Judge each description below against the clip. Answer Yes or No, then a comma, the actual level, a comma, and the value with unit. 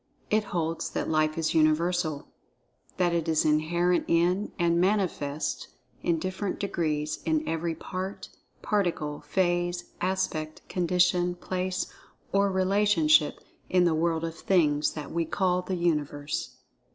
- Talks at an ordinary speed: No, slow, 125 wpm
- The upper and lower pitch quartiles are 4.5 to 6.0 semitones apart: No, average, 2.7 semitones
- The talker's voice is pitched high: No, medium, 170 Hz